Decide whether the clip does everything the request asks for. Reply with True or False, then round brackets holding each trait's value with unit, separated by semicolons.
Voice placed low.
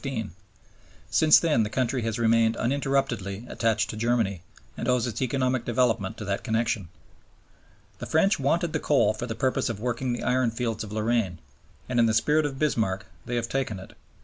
True (120 Hz)